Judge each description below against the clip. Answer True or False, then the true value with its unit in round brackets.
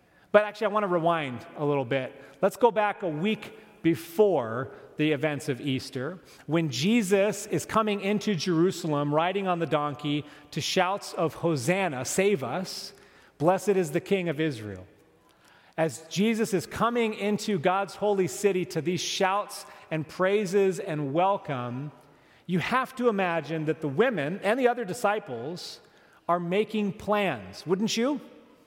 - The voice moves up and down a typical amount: True (4.8 semitones)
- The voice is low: False (185 Hz)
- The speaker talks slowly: False (150 wpm)